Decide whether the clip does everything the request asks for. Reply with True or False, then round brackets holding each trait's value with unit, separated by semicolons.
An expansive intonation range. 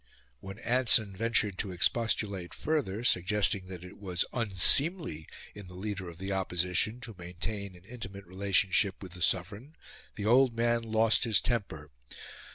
False (3.8 semitones)